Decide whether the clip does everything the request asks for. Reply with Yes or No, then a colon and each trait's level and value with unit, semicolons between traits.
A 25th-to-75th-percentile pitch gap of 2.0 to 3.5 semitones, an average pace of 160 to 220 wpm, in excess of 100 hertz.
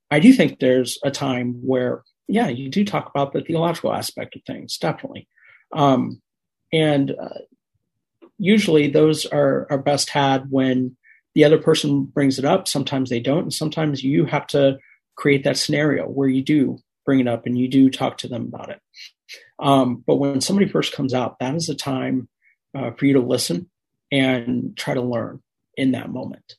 Yes: narrow, 2.4 semitones; average, 185 wpm; medium, 140 Hz